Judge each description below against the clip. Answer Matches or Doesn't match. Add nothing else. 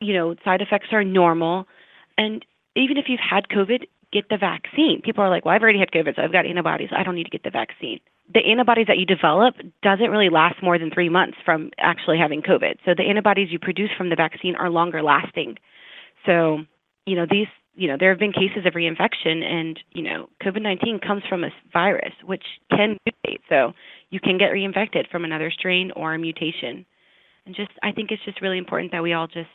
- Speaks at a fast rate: Matches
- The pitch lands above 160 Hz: Matches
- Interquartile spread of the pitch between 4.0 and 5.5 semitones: Doesn't match